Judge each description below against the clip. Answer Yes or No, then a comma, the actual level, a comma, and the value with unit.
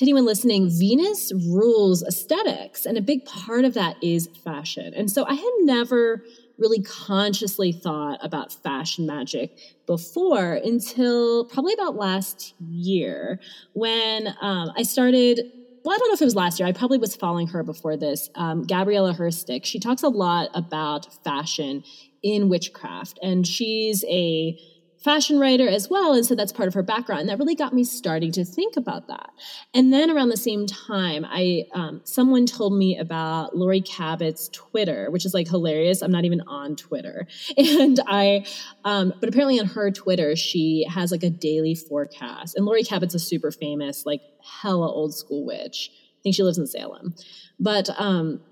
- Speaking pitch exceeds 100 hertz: Yes, high, 190 Hz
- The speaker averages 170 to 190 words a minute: Yes, average, 175 wpm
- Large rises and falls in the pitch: Yes, wide, 5.7 semitones